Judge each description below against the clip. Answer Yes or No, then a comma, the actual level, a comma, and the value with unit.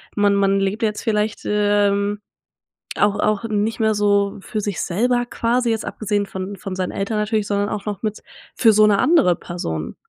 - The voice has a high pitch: Yes, high, 205 Hz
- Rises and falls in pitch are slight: Yes, narrow, 1.5 semitones